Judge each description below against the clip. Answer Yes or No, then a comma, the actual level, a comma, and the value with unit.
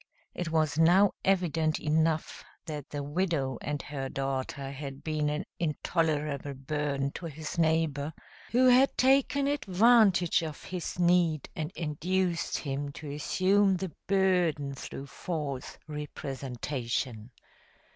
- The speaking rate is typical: No, slow, 120 wpm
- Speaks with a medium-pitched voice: Yes, medium, 155 Hz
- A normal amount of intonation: Yes, average, 4.0 semitones